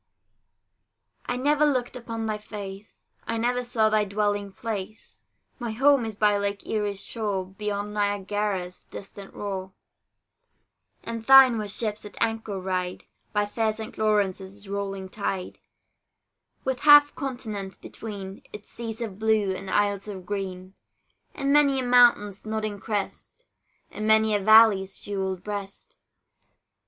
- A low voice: No, high, 210 Hz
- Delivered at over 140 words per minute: No, slow, 135 wpm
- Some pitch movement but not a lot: No, narrow, 2.3 semitones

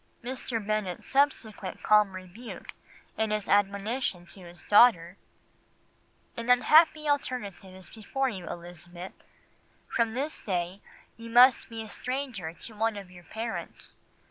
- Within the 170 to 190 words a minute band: No, slow, 135 wpm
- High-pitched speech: Yes, high, 215 Hz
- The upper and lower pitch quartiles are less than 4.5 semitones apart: No, average, 4.8 semitones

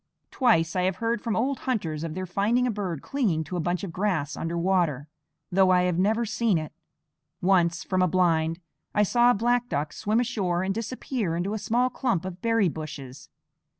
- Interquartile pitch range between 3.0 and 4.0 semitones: No, average, 5.3 semitones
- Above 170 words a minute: Yes, average, 200 wpm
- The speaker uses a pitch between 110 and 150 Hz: No, medium, 185 Hz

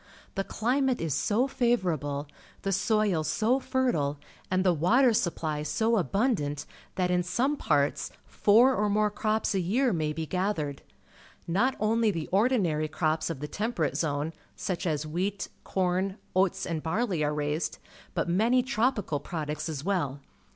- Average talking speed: Yes, average, 150 wpm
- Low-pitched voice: No, medium, 185 Hz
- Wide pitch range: Yes, wide, 6.0 semitones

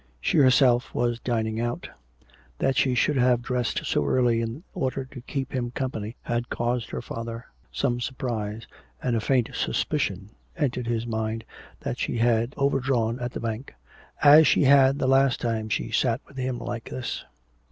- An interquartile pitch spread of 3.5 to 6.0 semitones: No, narrow, 2.4 semitones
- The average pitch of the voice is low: Yes, low, 120 Hz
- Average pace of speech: Yes, average, 170 wpm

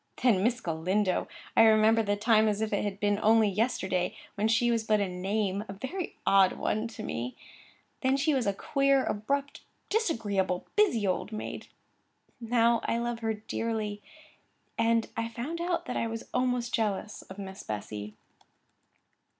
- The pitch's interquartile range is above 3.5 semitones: No, average, 2.9 semitones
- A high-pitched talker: Yes, high, 220 Hz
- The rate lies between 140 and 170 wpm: Yes, average, 160 wpm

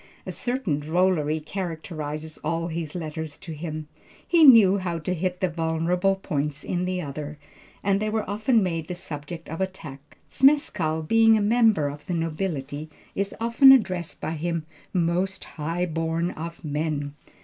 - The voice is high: No, medium, 170 Hz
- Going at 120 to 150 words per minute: No, average, 160 wpm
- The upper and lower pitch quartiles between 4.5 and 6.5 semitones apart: No, average, 3.6 semitones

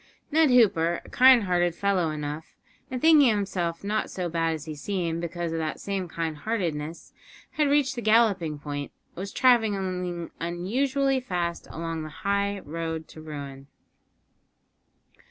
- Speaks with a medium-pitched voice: Yes, medium, 175 Hz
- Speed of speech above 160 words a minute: No, average, 150 wpm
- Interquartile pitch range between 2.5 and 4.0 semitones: No, average, 5.0 semitones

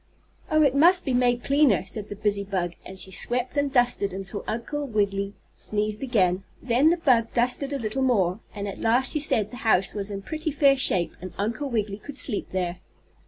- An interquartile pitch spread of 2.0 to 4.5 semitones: No, average, 5.3 semitones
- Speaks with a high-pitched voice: Yes, high, 225 Hz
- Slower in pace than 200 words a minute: No, fast, 205 wpm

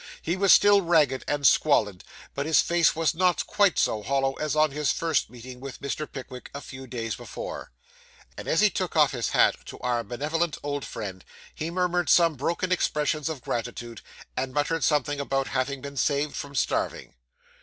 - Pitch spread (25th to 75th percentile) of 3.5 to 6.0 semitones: Yes, average, 4.0 semitones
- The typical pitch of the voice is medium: Yes, medium, 145 Hz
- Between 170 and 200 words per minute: Yes, average, 180 wpm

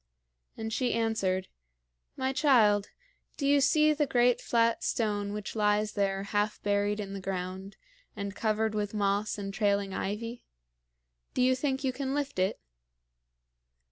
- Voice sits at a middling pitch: No, high, 210 Hz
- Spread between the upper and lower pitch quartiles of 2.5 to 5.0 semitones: Yes, average, 3.8 semitones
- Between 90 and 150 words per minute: Yes, average, 145 wpm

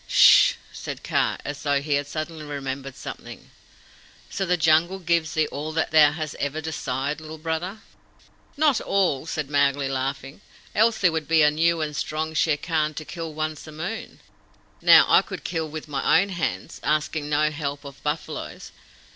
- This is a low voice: No, medium, 155 Hz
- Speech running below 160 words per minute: No, average, 175 wpm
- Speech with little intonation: Yes, narrow, 2.1 semitones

